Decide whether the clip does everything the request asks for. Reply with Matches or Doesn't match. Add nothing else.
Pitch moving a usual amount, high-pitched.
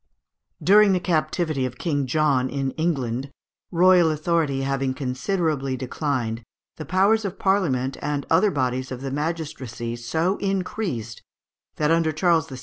Doesn't match